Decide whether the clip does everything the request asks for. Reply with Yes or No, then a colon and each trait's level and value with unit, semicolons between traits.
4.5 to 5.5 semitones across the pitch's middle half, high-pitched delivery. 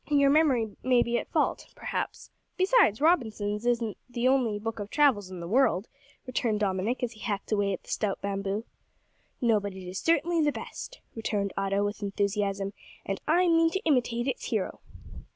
Yes: average, 5.2 semitones; high, 225 Hz